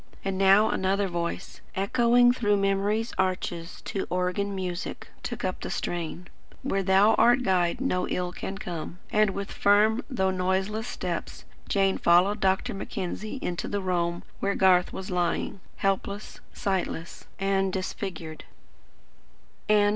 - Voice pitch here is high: Yes, high, 195 Hz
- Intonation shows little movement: Yes, narrow, 2.1 semitones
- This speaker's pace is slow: Yes, slow, 130 wpm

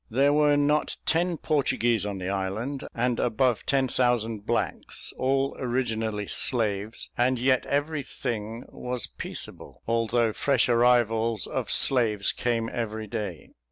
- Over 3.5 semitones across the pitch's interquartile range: No, average, 3.1 semitones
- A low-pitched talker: Yes, low, 120 Hz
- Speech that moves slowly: Yes, slow, 130 wpm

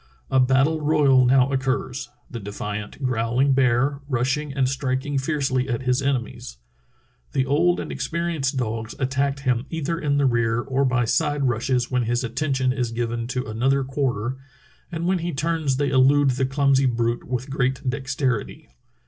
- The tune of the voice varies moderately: No, narrow, 2.2 semitones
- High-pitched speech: No, low, 130 Hz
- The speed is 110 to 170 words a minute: Yes, average, 165 wpm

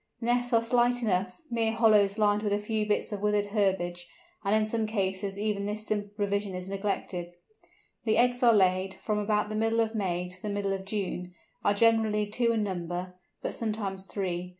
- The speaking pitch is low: No, high, 205 Hz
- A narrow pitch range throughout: Yes, narrow, 2.3 semitones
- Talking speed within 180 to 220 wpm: Yes, average, 200 wpm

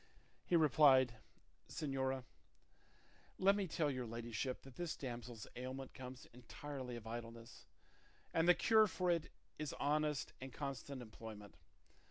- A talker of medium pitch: No, low, 130 Hz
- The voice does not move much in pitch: No, average, 4.2 semitones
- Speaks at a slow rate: Yes, slow, 130 wpm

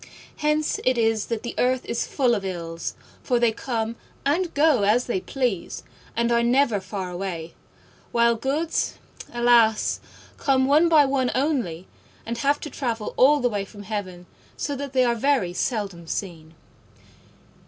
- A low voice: No, high, 235 Hz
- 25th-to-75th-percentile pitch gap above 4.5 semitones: Yes, average, 5.0 semitones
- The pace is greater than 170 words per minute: No, average, 160 wpm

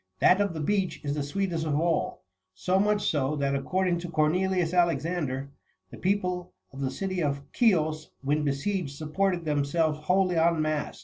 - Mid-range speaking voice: Yes, medium, 165 Hz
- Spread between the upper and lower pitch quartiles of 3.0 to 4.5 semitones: Yes, average, 3.8 semitones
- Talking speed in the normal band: Yes, average, 175 wpm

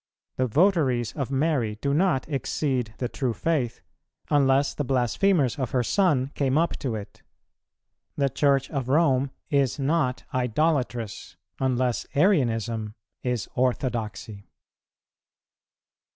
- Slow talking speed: Yes, slow, 115 wpm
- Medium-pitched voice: No, low, 130 Hz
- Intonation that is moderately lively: Yes, average, 3.2 semitones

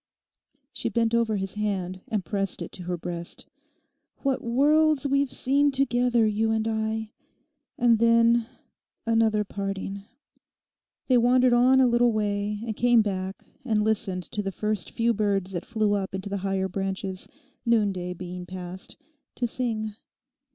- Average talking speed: Yes, average, 145 wpm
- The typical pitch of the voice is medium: No, high, 215 Hz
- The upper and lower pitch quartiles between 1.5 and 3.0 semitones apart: No, average, 3.4 semitones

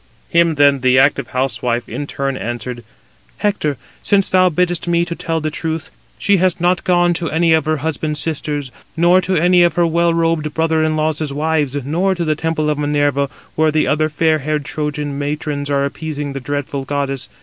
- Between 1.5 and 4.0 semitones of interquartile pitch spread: Yes, average, 2.7 semitones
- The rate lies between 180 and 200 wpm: Yes, average, 195 wpm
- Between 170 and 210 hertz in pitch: No, medium, 155 Hz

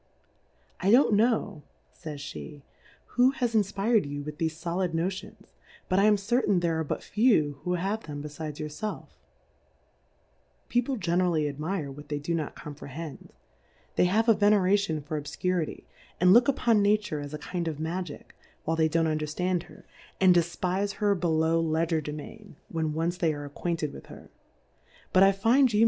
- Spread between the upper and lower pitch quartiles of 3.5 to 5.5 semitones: Yes, average, 4.8 semitones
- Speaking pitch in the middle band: Yes, medium, 170 Hz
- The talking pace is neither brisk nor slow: Yes, average, 180 wpm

